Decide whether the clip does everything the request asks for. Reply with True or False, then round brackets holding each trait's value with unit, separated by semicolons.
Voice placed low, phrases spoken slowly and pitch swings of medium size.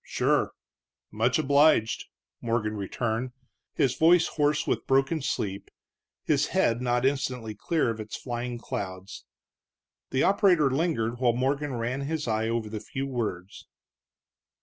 True (125 Hz; 130 wpm; 4.0 semitones)